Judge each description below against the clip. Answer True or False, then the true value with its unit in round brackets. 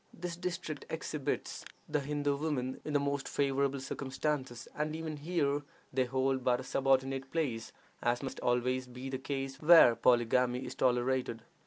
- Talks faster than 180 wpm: False (155 wpm)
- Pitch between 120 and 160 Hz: True (135 Hz)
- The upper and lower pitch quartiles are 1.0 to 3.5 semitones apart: True (2.6 semitones)